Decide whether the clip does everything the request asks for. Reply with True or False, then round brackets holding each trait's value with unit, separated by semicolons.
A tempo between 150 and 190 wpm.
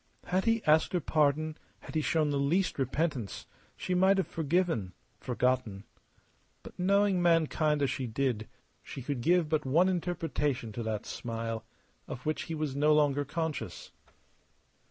True (155 wpm)